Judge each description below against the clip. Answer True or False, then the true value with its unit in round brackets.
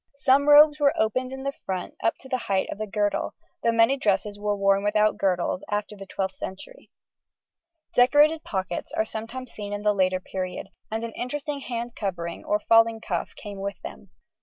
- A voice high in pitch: True (215 Hz)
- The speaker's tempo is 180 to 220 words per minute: True (190 wpm)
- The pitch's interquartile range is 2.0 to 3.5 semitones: False (4.5 semitones)